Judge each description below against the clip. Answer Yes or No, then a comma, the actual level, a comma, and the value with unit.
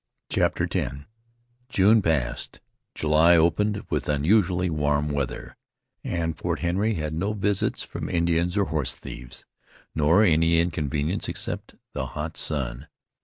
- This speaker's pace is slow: Yes, slow, 125 wpm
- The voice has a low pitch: Yes, very low, 80 Hz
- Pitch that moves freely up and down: No, average, 3.4 semitones